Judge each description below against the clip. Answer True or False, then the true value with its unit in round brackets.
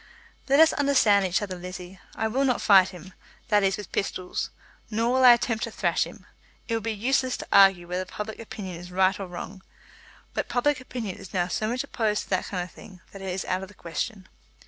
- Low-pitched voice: False (200 Hz)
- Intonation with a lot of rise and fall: False (3.8 semitones)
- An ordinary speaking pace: False (225 wpm)